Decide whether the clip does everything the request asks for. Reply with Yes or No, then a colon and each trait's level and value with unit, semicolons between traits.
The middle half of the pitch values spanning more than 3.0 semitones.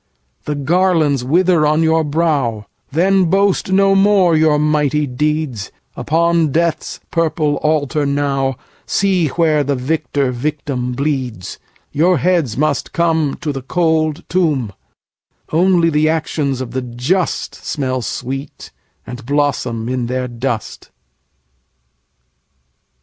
Yes: average, 3.9 semitones